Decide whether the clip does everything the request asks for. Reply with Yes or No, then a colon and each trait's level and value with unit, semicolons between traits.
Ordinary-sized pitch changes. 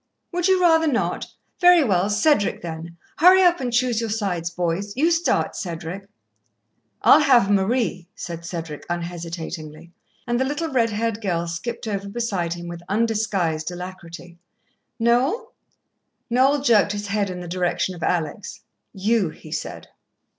No: wide, 5.9 semitones